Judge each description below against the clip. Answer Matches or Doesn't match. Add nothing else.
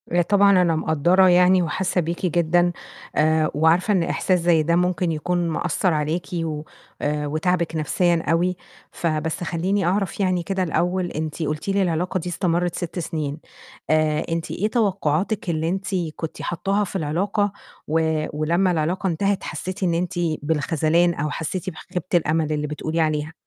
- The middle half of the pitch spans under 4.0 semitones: Matches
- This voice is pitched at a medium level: Matches